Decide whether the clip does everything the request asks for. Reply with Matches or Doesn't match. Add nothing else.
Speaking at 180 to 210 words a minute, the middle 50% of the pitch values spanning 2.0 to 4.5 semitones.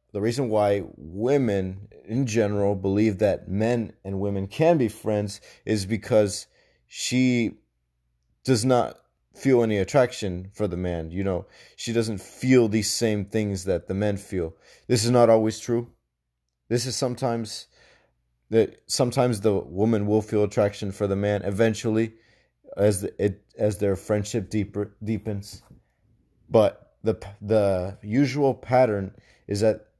Doesn't match